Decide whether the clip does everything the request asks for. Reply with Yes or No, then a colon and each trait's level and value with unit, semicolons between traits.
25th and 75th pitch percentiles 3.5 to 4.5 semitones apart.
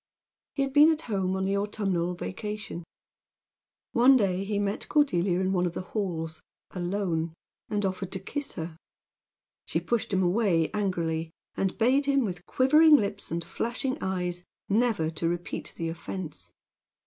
Yes: average, 4.2 semitones